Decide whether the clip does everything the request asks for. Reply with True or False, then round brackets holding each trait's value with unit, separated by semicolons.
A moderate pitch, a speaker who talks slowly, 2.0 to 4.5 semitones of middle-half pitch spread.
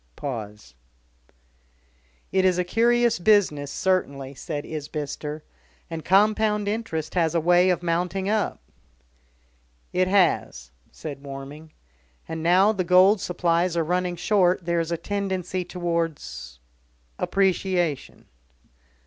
True (175 Hz; 110 wpm; 3.4 semitones)